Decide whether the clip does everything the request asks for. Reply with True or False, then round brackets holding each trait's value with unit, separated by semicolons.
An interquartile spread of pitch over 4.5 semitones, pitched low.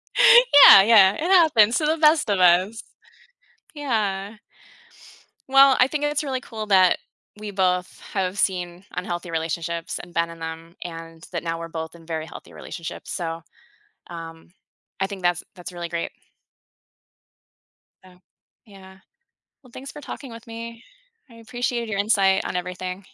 False (5.2 semitones; 190 Hz)